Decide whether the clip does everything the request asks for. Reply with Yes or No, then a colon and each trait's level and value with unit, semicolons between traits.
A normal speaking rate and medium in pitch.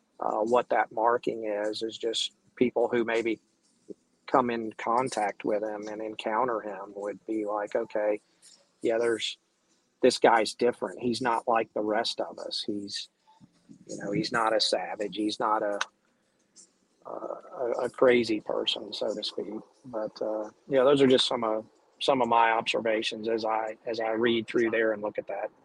No: average, 175 wpm; low, 110 Hz